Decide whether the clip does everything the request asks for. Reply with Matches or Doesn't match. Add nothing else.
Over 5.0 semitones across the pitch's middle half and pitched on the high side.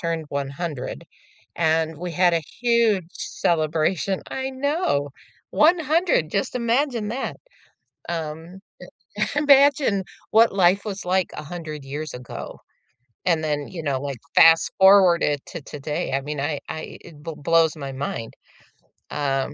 Doesn't match